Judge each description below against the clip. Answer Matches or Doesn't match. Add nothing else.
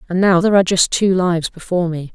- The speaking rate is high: Matches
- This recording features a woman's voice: Matches